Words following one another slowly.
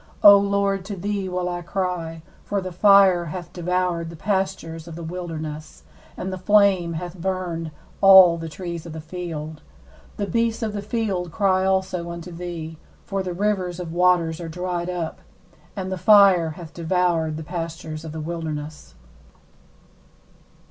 No: average, 160 wpm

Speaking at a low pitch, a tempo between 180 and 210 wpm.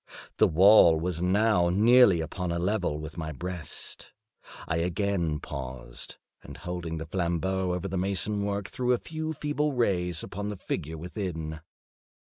No: very low, 90 Hz; average, 150 wpm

